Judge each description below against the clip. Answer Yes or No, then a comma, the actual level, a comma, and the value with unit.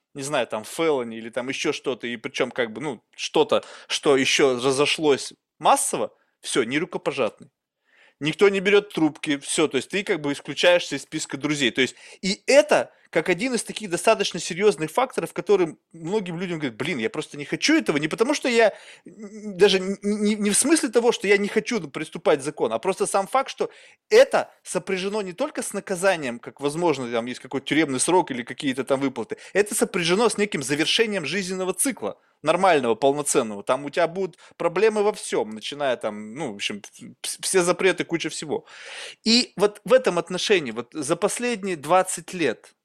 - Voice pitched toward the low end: No, medium, 185 Hz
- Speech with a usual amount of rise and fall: No, wide, 6.5 semitones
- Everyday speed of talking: No, fast, 185 wpm